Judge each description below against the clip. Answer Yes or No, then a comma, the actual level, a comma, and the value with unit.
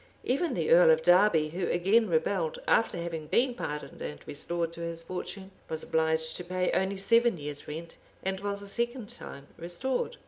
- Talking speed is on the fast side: No, average, 180 wpm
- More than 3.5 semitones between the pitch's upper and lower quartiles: Yes, average, 4.7 semitones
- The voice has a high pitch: No, medium, 180 Hz